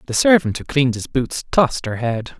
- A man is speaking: Yes, male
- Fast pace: Yes, fast, 225 wpm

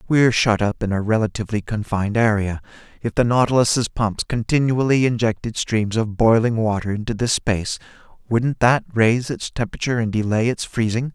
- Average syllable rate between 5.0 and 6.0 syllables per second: Yes, 5.7 syllables/s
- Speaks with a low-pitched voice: Yes, low, 115 Hz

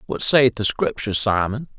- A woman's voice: No, male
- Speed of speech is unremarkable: Yes, average, 170 wpm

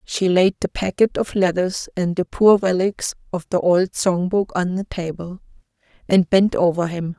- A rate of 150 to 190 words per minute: Yes, average, 185 wpm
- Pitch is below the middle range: No, medium, 185 Hz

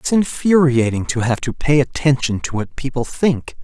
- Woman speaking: No, male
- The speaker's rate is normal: Yes, average, 180 wpm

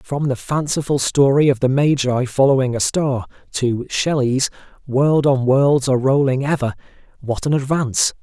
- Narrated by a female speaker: No, male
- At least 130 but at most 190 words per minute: Yes, average, 155 wpm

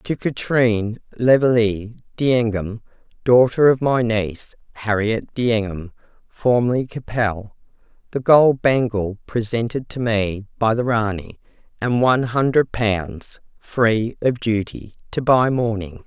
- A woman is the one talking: Yes, female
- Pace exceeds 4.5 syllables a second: No, 3.9 syllables/s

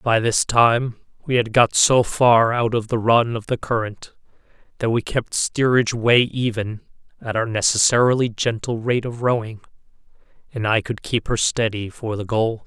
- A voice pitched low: Yes, low, 115 Hz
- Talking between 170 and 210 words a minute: Yes, average, 175 wpm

